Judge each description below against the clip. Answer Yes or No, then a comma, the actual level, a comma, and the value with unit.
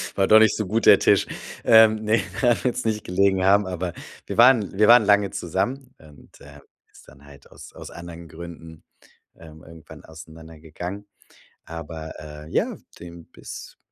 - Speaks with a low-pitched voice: Yes, very low, 90 Hz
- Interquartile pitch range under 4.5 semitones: No, average, 5.0 semitones